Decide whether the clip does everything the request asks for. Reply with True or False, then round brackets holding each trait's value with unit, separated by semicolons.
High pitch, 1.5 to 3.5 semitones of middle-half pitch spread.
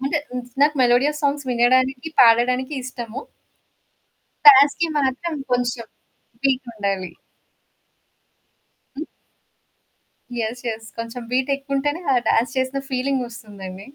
True (255 Hz; 2.9 semitones)